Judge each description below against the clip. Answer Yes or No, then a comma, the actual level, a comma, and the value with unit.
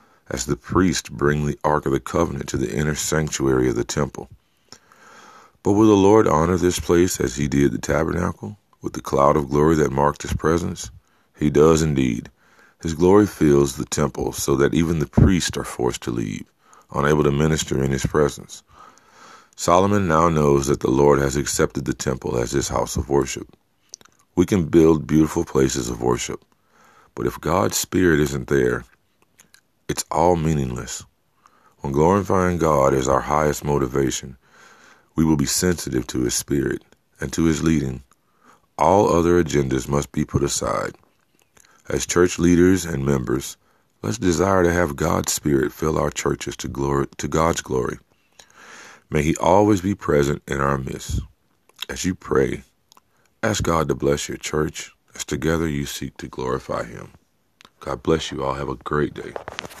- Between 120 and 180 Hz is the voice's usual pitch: No, very low, 75 Hz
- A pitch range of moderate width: Yes, average, 3.8 semitones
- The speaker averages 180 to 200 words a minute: No, average, 170 wpm